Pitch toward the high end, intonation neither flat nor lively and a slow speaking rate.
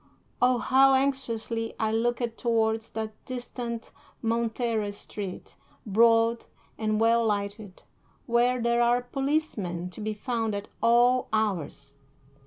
No: high, 230 Hz; narrow, 2.0 semitones; slow, 115 wpm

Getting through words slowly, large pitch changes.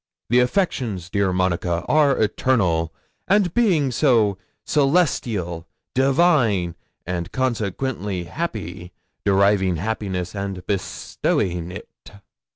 Yes: slow, 90 wpm; wide, 6.5 semitones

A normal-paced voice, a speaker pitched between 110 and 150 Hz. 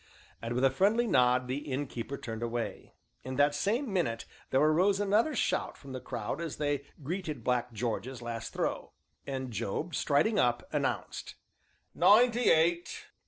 Yes: average, 155 wpm; medium, 140 Hz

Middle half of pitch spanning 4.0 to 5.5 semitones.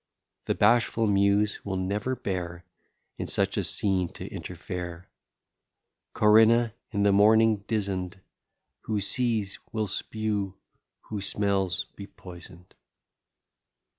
No: narrow, 2.6 semitones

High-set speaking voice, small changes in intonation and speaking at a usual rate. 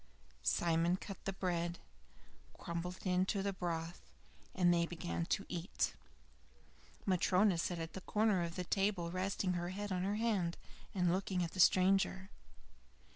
No: medium, 180 Hz; narrow, 2.1 semitones; average, 150 wpm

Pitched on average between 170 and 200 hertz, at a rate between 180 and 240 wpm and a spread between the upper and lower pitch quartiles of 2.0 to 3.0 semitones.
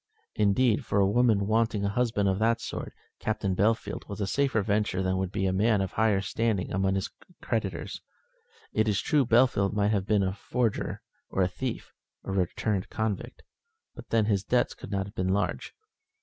No: low, 105 Hz; average, 190 wpm; narrow, 2.5 semitones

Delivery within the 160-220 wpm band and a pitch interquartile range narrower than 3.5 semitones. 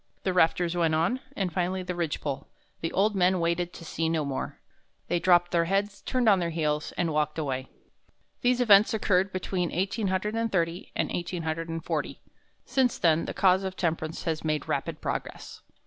Yes: average, 170 wpm; average, 2.7 semitones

